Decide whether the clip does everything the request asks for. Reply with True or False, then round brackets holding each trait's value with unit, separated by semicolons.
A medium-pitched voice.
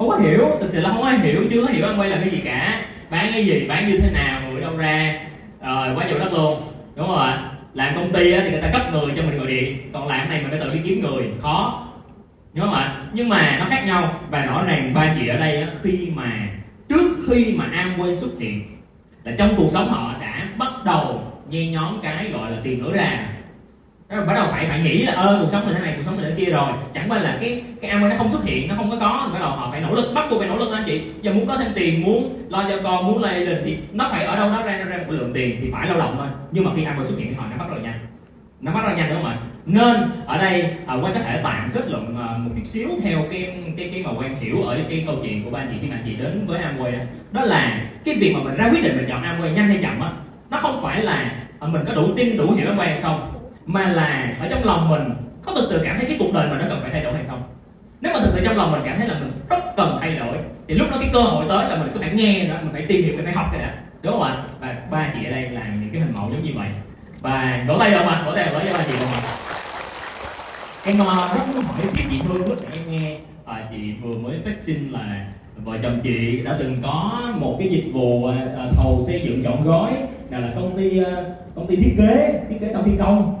True (165 Hz)